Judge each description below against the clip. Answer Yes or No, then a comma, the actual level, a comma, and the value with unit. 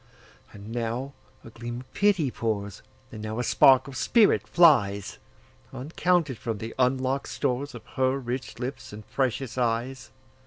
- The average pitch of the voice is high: No, low, 125 Hz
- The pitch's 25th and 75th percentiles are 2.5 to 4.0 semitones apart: Yes, average, 2.9 semitones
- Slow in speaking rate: Yes, slow, 130 wpm